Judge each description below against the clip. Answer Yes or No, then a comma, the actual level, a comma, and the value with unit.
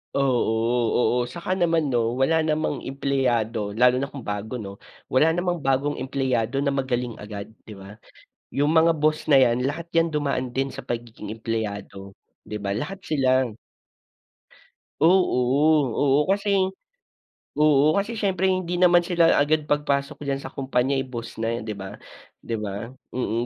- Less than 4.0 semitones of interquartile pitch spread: No, average, 4.9 semitones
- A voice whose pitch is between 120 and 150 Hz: Yes, low, 135 Hz